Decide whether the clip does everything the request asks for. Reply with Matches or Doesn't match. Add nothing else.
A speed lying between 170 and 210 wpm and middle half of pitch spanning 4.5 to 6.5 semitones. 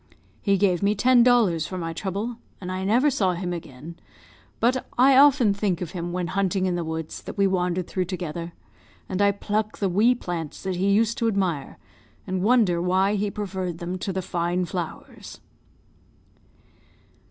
Doesn't match